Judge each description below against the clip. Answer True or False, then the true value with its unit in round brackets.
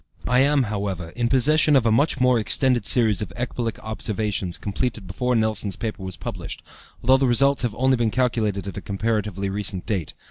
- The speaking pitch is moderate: False (110 Hz)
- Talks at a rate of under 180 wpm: False (185 wpm)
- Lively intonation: False (3.9 semitones)